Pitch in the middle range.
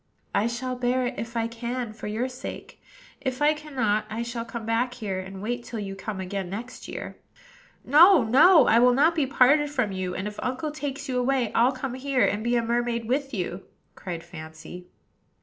No: high, 240 Hz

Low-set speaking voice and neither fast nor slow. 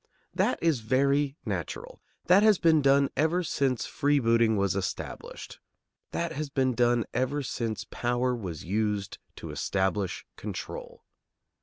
No: low, 125 Hz; slow, 130 wpm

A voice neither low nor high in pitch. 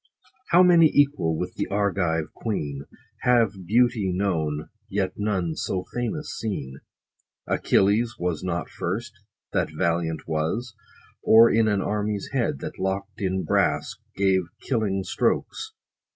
No: low, 100 Hz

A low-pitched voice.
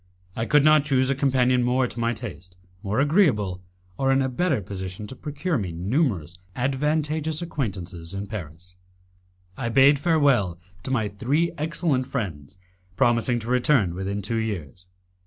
Yes: low, 125 Hz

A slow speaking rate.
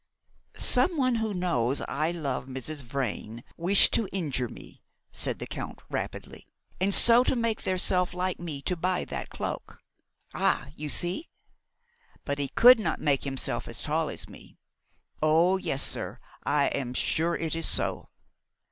No: average, 155 wpm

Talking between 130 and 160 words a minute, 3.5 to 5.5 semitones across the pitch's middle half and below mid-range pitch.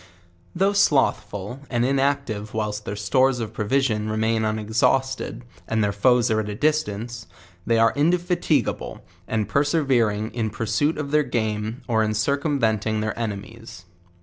Yes: average, 145 wpm; average, 4.2 semitones; low, 115 Hz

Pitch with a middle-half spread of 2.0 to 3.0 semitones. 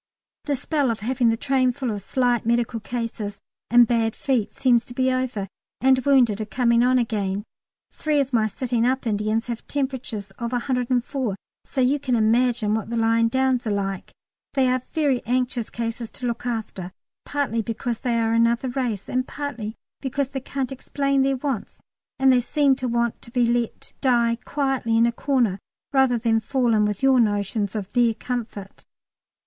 Yes: narrow, 2.5 semitones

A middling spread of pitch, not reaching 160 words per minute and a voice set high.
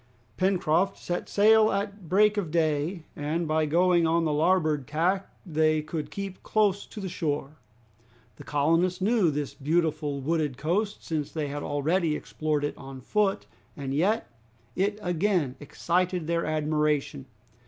No: average, 3.8 semitones; average, 145 wpm; medium, 165 Hz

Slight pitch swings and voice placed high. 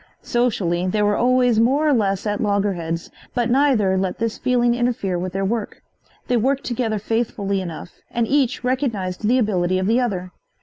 No: average, 4.5 semitones; high, 215 Hz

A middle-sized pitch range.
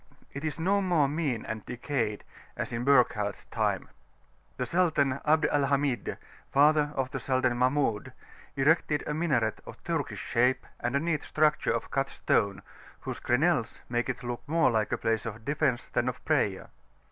Yes: average, 4.0 semitones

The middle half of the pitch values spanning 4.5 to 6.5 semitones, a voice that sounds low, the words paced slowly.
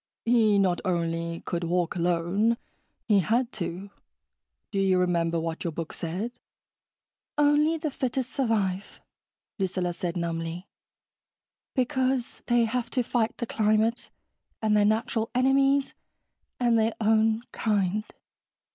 No: average, 5.2 semitones; high, 215 Hz; slow, 120 wpm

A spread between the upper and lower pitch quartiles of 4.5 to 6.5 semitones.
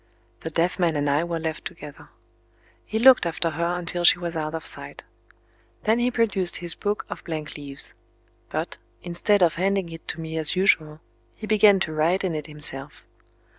No: average, 3.4 semitones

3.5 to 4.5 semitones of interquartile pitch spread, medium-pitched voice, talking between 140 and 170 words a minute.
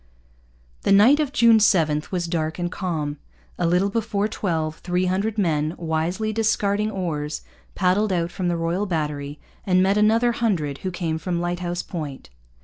Yes: average, 4.1 semitones; medium, 180 Hz; average, 160 wpm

